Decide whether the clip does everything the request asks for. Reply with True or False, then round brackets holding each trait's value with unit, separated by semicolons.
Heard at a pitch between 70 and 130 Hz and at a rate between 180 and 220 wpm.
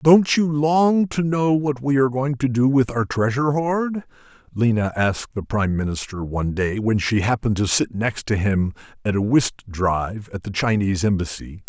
True (120 Hz; 195 wpm)